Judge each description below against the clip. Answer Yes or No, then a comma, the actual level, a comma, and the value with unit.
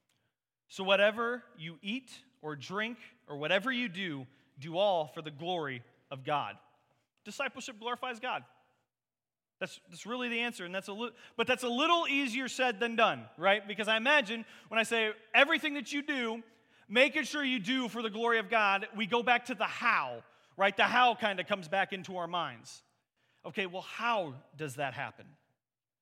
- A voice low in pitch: No, high, 215 Hz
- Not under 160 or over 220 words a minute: Yes, average, 180 wpm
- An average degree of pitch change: No, wide, 6.2 semitones